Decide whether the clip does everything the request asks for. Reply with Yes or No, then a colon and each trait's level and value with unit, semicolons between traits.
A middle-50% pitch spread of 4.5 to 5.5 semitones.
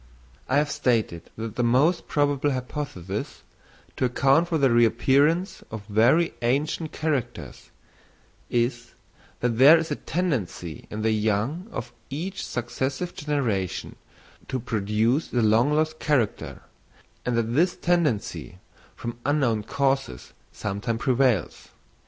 Yes: average, 4.9 semitones